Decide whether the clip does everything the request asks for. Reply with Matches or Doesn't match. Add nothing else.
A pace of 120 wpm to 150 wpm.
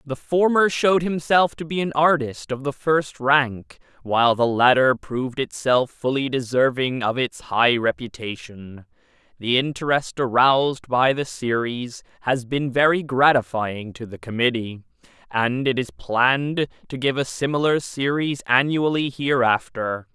Matches